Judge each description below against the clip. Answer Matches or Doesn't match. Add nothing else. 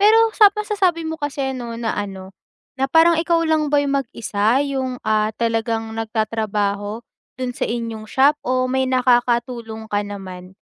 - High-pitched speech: Matches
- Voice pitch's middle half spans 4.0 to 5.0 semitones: Matches